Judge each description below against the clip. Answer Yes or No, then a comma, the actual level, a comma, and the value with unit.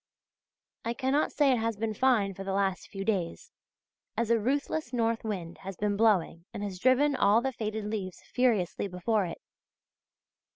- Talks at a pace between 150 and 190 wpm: Yes, average, 170 wpm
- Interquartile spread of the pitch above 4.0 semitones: No, average, 3.7 semitones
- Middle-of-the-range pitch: No, high, 215 Hz